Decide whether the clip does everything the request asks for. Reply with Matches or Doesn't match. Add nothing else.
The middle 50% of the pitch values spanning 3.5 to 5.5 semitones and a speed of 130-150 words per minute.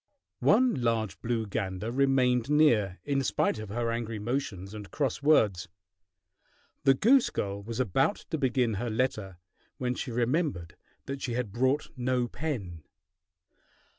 Matches